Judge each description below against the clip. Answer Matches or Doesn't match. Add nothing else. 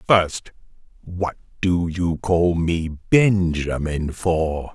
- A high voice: Doesn't match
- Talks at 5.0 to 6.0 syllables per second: Doesn't match